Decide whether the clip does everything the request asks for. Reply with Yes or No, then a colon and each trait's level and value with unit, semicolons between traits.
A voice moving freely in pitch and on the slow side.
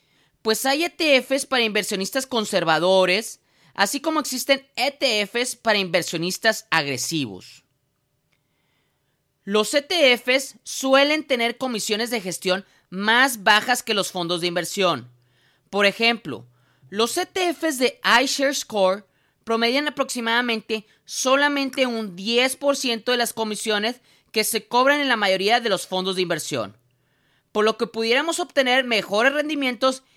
Yes: wide, 5.8 semitones; slow, 120 wpm